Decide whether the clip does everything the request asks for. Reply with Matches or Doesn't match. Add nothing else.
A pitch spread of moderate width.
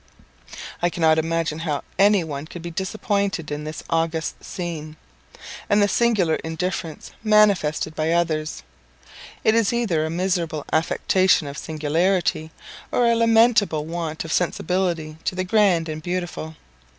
Matches